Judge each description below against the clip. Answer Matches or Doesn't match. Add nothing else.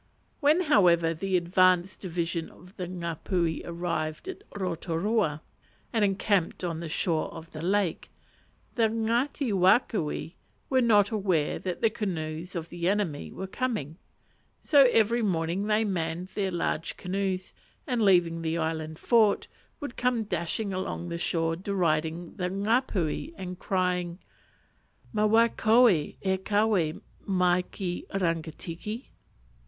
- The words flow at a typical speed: Doesn't match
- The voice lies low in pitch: Doesn't match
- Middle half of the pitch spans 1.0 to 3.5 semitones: Doesn't match